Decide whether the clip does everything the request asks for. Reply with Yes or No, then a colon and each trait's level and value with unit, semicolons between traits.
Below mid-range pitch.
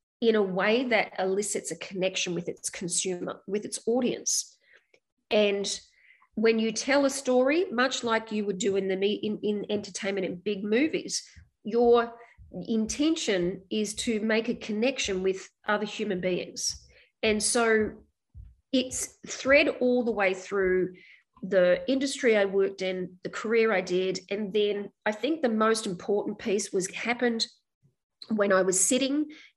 No: high, 215 Hz